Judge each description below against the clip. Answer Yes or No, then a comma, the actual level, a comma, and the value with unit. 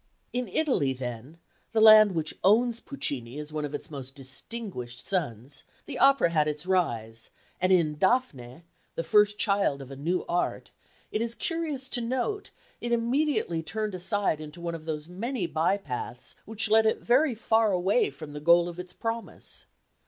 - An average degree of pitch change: No, wide, 7.3 semitones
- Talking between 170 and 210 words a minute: Yes, average, 175 wpm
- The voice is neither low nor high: Yes, medium, 180 Hz